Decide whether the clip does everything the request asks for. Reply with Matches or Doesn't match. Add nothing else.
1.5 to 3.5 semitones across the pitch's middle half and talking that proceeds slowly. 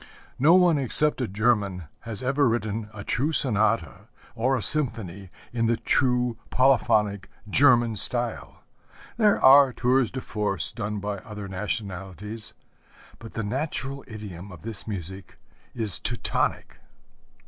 Doesn't match